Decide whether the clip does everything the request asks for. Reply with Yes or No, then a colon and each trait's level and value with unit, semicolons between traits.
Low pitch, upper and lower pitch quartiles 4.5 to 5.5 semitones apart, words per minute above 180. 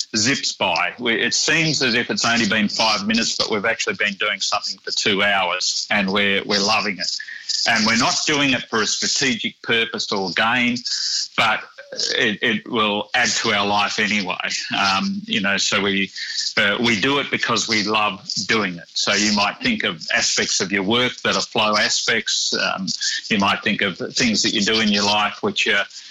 Yes: low, 115 Hz; average, 4.8 semitones; average, 200 wpm